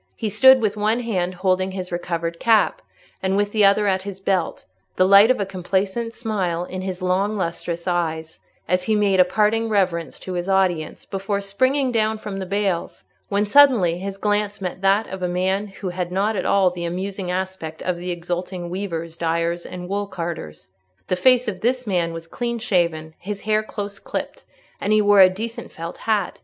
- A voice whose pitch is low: No, high, 190 Hz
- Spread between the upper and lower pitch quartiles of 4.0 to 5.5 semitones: No, average, 2.7 semitones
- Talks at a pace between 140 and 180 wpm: No, average, 190 wpm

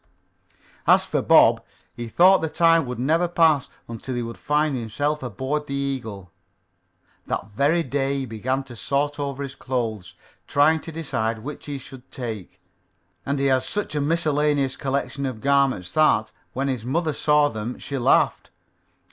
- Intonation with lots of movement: No, average, 3.4 semitones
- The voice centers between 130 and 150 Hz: Yes, medium, 140 Hz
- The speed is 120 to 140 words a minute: No, average, 165 wpm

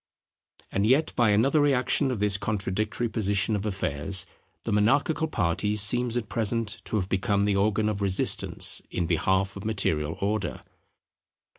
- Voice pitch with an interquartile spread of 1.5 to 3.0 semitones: Yes, average, 2.7 semitones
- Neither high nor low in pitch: No, low, 105 Hz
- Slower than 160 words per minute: Yes, average, 150 wpm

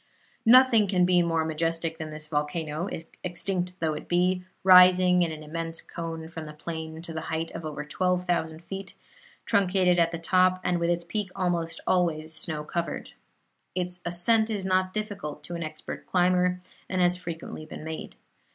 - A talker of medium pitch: Yes, medium, 175 Hz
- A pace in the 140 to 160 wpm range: No, average, 175 wpm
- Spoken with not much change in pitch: Yes, narrow, 2.2 semitones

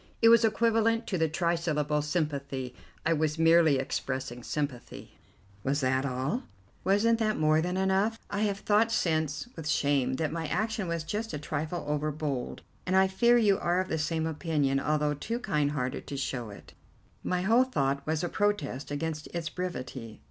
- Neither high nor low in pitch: Yes, medium, 160 Hz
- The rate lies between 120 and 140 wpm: No, average, 175 wpm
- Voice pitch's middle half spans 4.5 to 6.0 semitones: Yes, average, 5.1 semitones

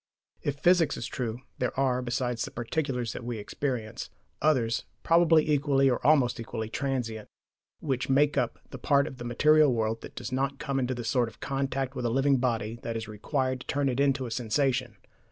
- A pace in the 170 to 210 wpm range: Yes, average, 195 wpm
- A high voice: No, low, 130 Hz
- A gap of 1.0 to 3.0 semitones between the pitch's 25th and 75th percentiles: Yes, average, 2.7 semitones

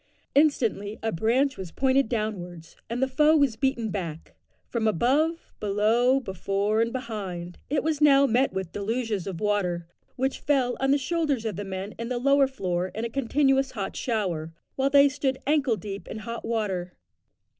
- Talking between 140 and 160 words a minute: No, average, 175 wpm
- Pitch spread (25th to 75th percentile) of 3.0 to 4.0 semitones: No, wide, 5.4 semitones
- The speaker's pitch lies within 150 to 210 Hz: No, high, 230 Hz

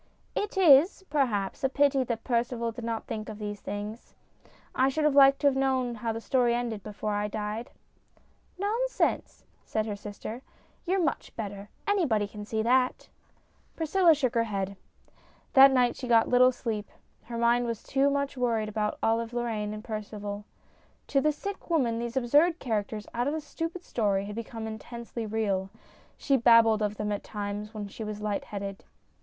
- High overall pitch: Yes, high, 230 Hz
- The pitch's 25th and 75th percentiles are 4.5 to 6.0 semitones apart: No, average, 4.1 semitones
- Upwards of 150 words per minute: Yes, average, 185 wpm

